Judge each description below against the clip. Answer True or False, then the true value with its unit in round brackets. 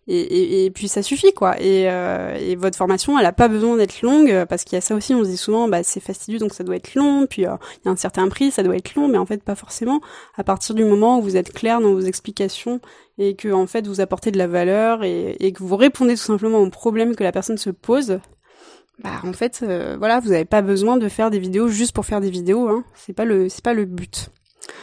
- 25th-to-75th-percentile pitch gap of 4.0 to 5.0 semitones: False (3.6 semitones)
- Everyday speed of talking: False (275 wpm)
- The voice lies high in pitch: True (210 Hz)